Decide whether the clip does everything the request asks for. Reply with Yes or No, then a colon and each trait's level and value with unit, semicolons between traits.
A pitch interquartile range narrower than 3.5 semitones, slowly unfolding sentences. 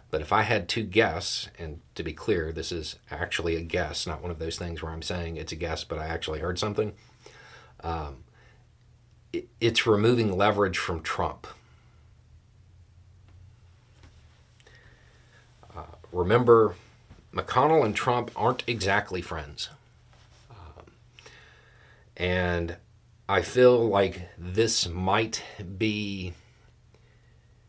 No: average, 4.5 semitones; slow, 115 wpm